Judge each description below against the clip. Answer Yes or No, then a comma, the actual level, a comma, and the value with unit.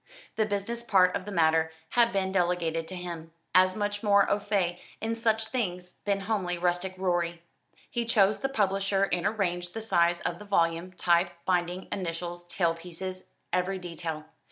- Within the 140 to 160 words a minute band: No, average, 170 wpm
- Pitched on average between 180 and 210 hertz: Yes, medium, 185 Hz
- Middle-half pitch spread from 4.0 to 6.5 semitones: No, average, 2.7 semitones